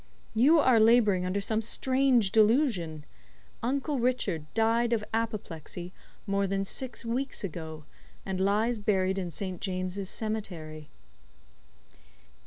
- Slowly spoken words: Yes, slow, 120 wpm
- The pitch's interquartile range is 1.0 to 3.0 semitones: No, average, 4.1 semitones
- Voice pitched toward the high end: Yes, high, 205 Hz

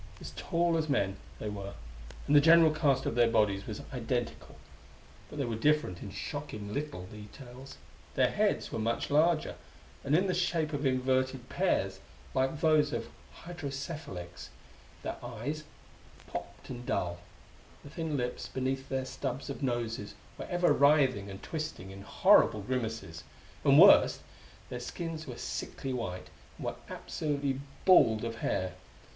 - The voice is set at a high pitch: No, low, 130 Hz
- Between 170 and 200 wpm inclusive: No, average, 150 wpm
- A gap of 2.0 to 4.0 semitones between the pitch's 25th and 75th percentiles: No, average, 5.3 semitones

